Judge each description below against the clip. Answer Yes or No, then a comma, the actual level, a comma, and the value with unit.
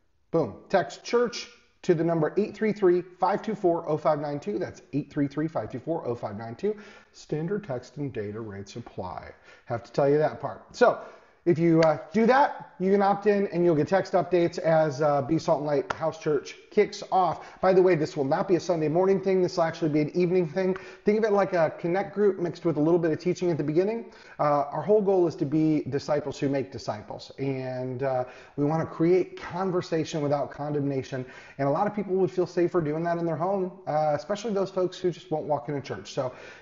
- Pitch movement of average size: Yes, average, 4.2 semitones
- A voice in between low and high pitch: Yes, medium, 165 Hz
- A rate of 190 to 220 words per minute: Yes, fast, 205 wpm